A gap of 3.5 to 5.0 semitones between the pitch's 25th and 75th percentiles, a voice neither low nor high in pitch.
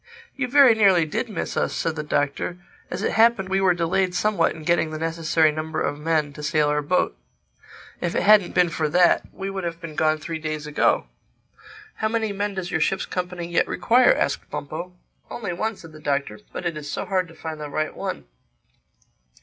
Yes: average, 3.8 semitones; medium, 170 Hz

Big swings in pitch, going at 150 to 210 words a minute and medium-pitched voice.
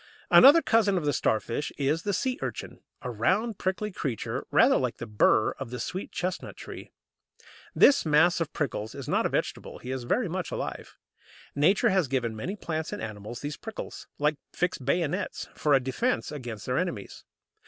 Yes: wide, 7.2 semitones; average, 180 wpm; medium, 150 Hz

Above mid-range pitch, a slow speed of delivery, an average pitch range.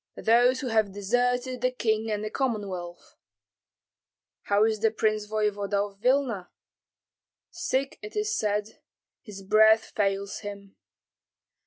Yes: high, 215 Hz; slow, 125 wpm; average, 3.3 semitones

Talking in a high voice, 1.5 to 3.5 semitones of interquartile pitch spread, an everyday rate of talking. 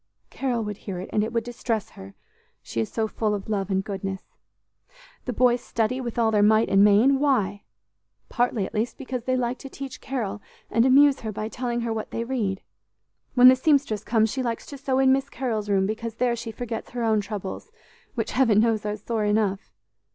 No: high, 225 Hz; average, 3.2 semitones; fast, 210 wpm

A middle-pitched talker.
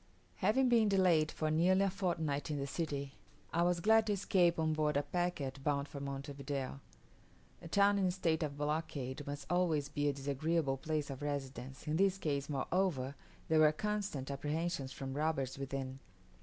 Yes: medium, 150 Hz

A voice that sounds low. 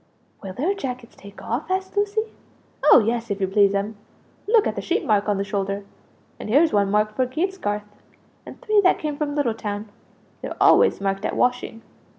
No: high, 230 Hz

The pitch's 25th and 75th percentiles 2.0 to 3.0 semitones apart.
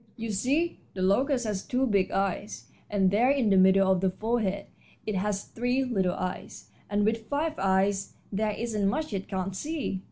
No: average, 4.1 semitones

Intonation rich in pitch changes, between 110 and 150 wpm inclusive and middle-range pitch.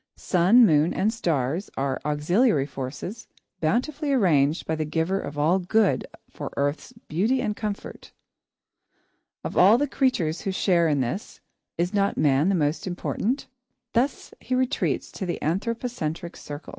Yes: wide, 6.6 semitones; average, 145 wpm; medium, 180 Hz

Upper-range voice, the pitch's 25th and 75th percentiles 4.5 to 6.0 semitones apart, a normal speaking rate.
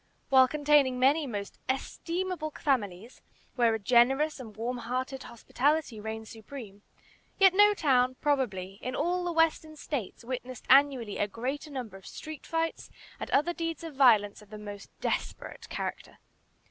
Yes: very high, 260 Hz; average, 5.3 semitones; average, 150 wpm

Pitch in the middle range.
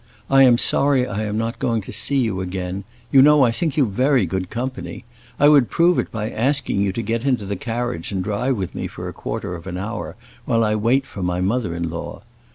No: low, 115 Hz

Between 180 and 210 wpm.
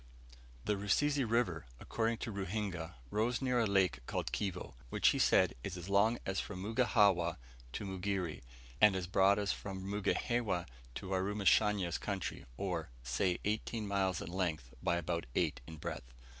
No: average, 155 wpm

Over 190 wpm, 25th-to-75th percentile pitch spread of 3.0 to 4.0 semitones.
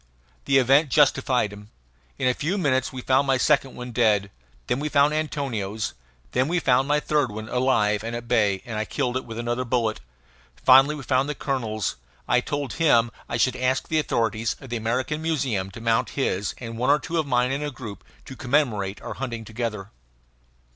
Yes: average, 200 wpm; average, 3.6 semitones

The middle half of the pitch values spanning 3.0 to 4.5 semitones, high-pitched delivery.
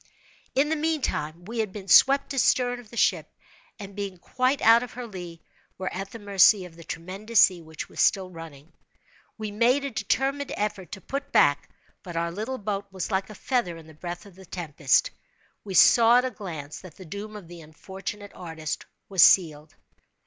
No: average, 5.2 semitones; high, 195 Hz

